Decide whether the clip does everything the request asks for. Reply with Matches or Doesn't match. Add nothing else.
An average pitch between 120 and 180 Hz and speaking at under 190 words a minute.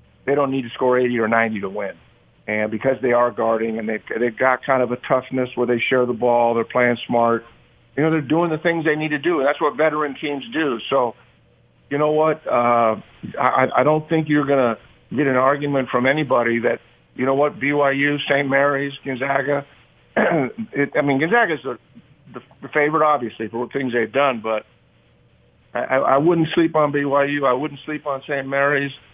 Doesn't match